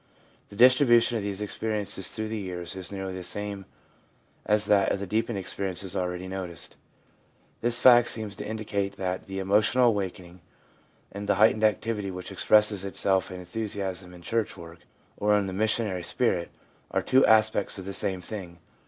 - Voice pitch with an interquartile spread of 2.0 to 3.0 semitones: Yes, average, 2.7 semitones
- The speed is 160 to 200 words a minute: Yes, average, 170 wpm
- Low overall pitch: Yes, low, 100 Hz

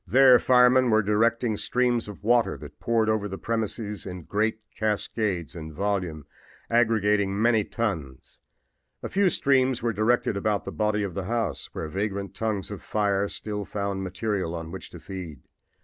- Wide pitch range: No, average, 3.0 semitones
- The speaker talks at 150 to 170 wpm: Yes, average, 165 wpm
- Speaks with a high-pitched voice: No, low, 105 Hz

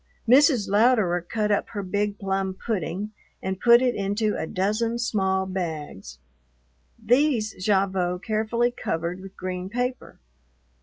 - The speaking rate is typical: No, slow, 125 wpm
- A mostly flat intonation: No, average, 3.6 semitones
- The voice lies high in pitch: Yes, high, 200 Hz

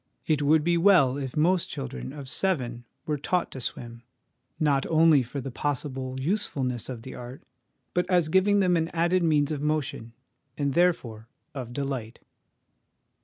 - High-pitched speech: No, medium, 145 Hz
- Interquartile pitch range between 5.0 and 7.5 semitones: No, average, 4.5 semitones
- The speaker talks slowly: No, average, 165 wpm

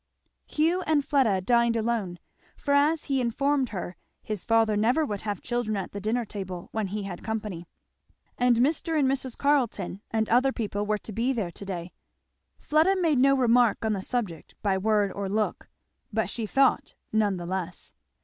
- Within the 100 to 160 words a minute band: No, average, 180 wpm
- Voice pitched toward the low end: No, high, 220 Hz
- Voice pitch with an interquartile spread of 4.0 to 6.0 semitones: Yes, average, 4.6 semitones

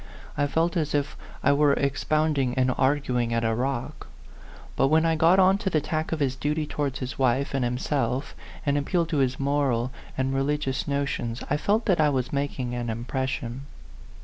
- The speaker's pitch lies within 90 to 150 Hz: Yes, medium, 140 Hz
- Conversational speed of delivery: Yes, average, 190 wpm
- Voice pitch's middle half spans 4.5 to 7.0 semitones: No, average, 2.8 semitones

